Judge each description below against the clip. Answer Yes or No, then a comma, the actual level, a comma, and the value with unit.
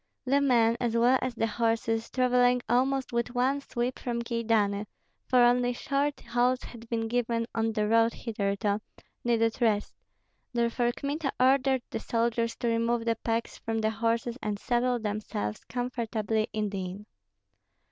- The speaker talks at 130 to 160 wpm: Yes, average, 155 wpm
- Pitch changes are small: Yes, narrow, 1.7 semitones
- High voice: Yes, high, 235 Hz